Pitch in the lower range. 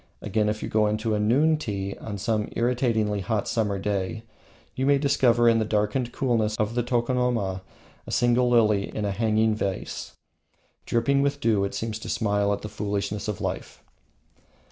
Yes: low, 110 Hz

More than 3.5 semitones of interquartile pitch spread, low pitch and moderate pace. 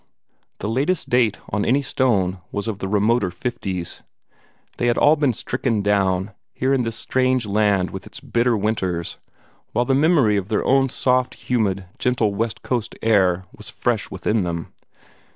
Yes: average, 4.3 semitones; low, 110 Hz; average, 165 wpm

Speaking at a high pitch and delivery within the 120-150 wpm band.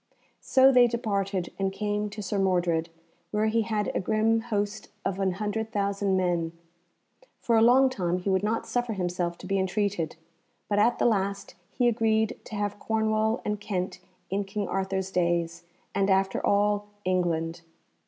No: high, 200 Hz; average, 165 wpm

